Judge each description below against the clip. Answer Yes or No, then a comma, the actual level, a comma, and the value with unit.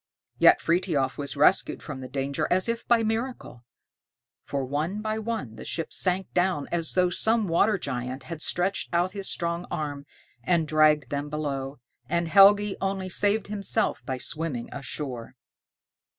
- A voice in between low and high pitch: Yes, medium, 170 Hz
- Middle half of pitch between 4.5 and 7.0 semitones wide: Yes, wide, 5.5 semitones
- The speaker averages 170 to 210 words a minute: No, average, 155 wpm